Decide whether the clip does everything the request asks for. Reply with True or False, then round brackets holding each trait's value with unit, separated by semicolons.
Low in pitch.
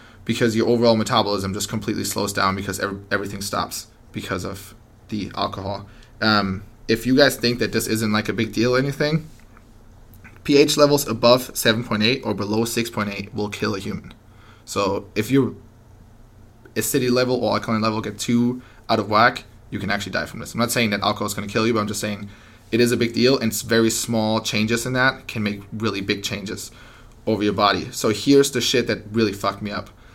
True (110 Hz)